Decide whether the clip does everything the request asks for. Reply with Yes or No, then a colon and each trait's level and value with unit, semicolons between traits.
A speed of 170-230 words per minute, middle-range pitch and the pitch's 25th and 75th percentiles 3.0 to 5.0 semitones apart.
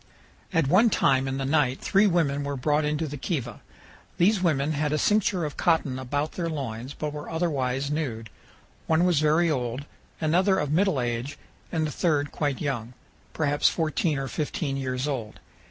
Yes: average, 175 wpm; medium, 150 Hz; average, 3.3 semitones